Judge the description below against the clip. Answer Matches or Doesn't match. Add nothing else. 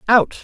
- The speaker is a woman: Doesn't match